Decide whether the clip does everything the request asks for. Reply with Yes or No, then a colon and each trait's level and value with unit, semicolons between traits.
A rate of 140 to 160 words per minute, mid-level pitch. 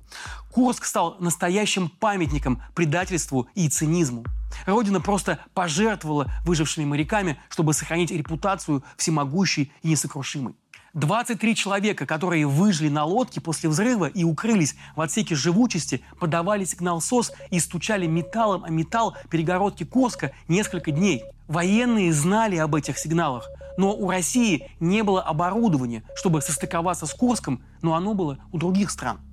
No: average, 130 wpm; medium, 170 Hz